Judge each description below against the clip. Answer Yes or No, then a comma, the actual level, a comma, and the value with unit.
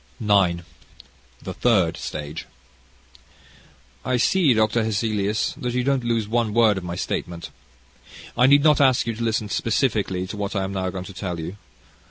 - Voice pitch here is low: Yes, low, 110 Hz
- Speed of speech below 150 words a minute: No, average, 175 wpm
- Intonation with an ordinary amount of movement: Yes, average, 4.0 semitones